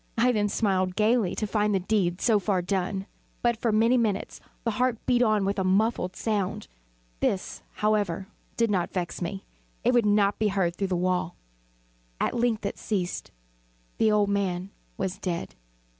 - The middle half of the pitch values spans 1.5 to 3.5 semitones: Yes, average, 2.9 semitones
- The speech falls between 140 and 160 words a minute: No, average, 175 wpm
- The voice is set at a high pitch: Yes, high, 205 Hz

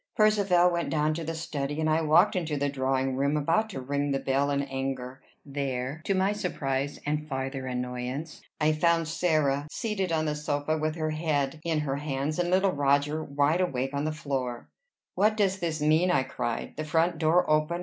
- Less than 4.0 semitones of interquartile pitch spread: Yes, average, 3.2 semitones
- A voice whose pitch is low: No, medium, 150 Hz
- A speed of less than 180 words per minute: No, average, 195 wpm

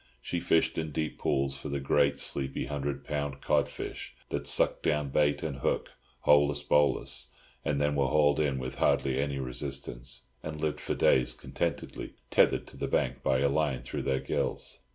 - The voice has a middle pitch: No, very low, 70 Hz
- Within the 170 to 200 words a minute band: Yes, average, 180 wpm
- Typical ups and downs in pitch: No, narrow, 1.5 semitones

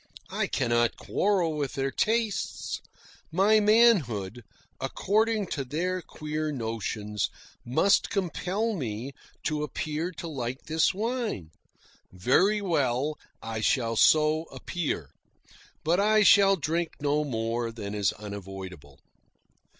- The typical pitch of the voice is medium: Yes, medium, 150 Hz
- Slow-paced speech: Yes, slow, 110 wpm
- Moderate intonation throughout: No, wide, 8.6 semitones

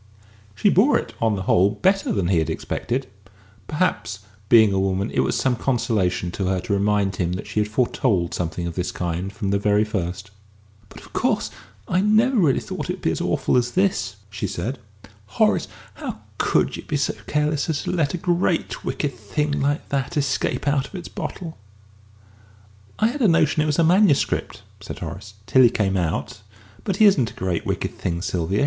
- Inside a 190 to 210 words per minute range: Yes, average, 200 wpm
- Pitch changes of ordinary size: No, wide, 7.8 semitones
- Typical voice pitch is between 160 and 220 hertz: No, low, 110 Hz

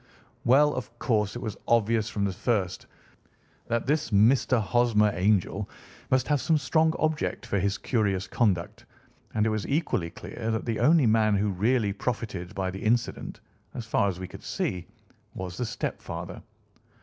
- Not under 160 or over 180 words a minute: Yes, average, 165 wpm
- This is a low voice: Yes, low, 110 Hz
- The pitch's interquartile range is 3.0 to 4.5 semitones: Yes, average, 3.6 semitones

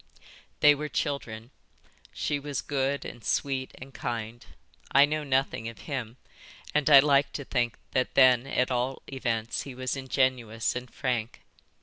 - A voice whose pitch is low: Yes, low, 130 Hz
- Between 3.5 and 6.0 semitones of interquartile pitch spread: No, narrow, 2.6 semitones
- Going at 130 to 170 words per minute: Yes, average, 150 wpm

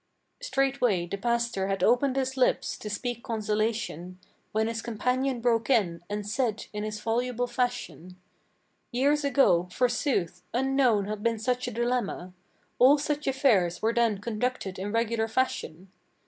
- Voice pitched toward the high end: Yes, high, 230 Hz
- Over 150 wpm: No, average, 145 wpm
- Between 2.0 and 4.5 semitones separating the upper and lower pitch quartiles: Yes, average, 3.4 semitones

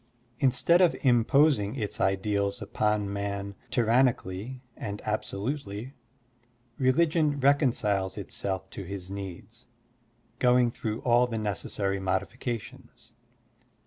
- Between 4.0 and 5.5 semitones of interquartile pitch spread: Yes, average, 4.3 semitones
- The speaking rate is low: Yes, slow, 100 wpm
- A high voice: No, low, 110 Hz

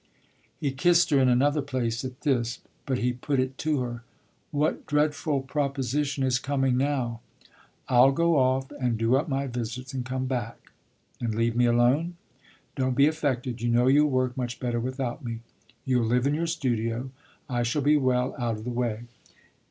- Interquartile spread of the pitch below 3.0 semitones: Yes, narrow, 2.6 semitones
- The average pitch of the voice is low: Yes, low, 130 Hz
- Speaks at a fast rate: No, average, 180 wpm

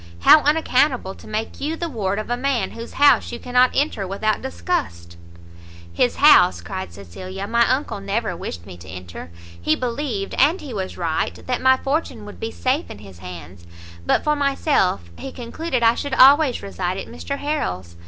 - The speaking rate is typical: Yes, average, 185 wpm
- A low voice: No, high, 225 Hz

